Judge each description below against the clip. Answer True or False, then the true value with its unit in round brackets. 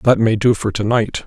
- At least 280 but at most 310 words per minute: True (285 wpm)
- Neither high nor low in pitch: False (110 Hz)